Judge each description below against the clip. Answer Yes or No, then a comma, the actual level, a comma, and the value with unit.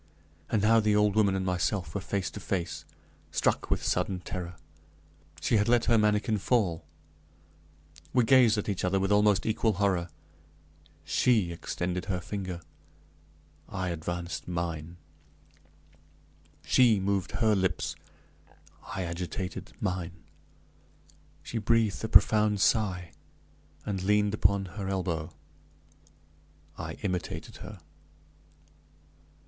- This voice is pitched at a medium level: No, very low, 95 Hz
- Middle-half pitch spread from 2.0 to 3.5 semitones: Yes, average, 2.9 semitones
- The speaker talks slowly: Yes, slow, 115 wpm